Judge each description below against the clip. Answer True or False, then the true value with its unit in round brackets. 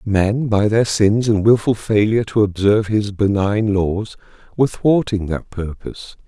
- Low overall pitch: True (105 Hz)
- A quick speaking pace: False (155 wpm)